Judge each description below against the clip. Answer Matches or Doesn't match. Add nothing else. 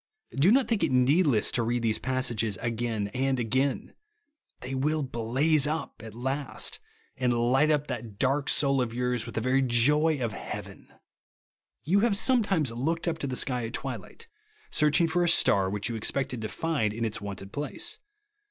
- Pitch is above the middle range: Doesn't match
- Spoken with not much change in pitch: Doesn't match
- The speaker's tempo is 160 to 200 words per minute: Matches